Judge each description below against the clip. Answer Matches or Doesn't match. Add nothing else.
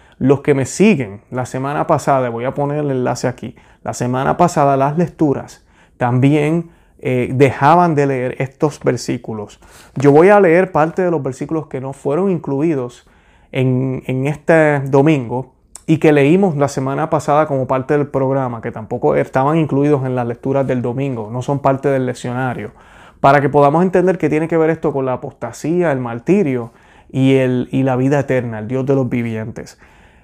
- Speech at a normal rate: Matches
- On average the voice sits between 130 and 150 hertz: Matches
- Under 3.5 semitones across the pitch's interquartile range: Matches